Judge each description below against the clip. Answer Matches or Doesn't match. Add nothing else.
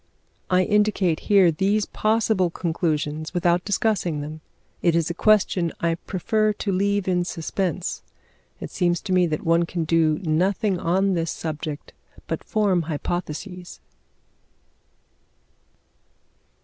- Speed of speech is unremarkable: Doesn't match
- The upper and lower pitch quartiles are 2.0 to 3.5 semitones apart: Matches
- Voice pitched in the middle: Matches